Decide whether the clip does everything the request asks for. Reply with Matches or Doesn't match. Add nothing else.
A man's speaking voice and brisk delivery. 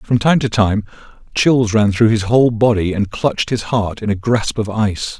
Matches